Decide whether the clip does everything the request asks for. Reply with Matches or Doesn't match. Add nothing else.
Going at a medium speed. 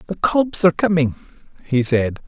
Matches